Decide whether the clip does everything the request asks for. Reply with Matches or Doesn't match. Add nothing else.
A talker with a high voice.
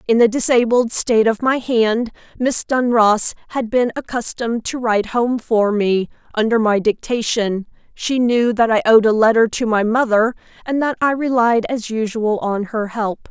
Matches